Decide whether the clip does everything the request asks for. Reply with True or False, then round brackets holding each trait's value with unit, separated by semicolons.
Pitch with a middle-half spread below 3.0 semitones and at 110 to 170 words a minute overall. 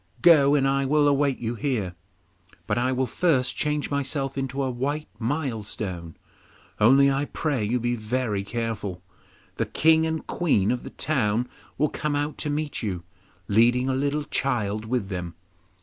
False (4.5 semitones; 165 wpm)